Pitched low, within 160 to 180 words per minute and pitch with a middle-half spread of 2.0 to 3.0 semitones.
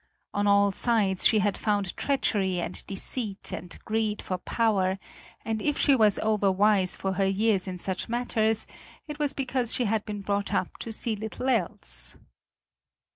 No: high, 210 Hz; average, 165 wpm; narrow, 2.6 semitones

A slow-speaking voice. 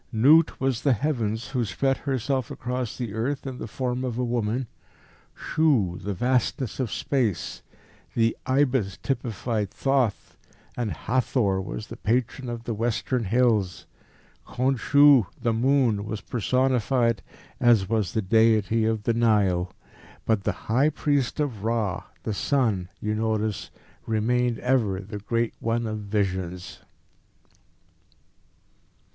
Yes: slow, 130 wpm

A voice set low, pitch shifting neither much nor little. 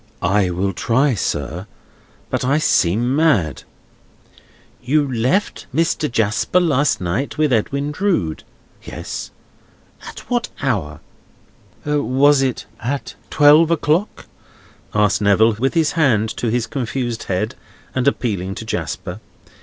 No: low, 125 Hz; wide, 6.3 semitones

